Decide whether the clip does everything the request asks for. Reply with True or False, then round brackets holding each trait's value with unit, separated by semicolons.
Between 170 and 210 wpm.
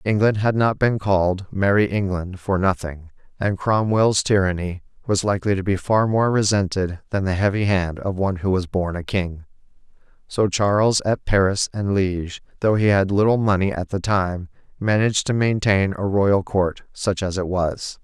True (180 wpm)